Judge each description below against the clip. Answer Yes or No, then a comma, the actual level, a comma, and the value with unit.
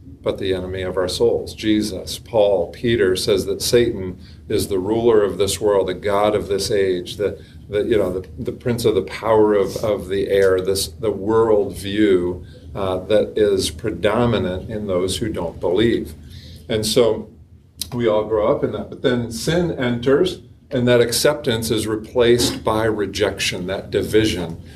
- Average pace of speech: Yes, average, 170 wpm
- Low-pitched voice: Yes, low, 105 Hz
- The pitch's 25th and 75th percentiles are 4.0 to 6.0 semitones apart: Yes, average, 4.4 semitones